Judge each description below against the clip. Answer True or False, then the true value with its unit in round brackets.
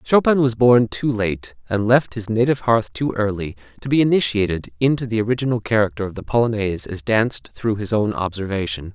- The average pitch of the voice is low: True (110 Hz)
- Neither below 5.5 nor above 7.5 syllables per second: True (5.7 syllables/s)